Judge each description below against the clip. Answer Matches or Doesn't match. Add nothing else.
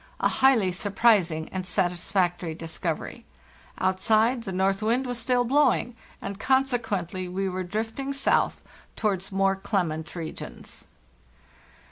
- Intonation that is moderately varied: Matches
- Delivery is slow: Matches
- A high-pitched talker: Matches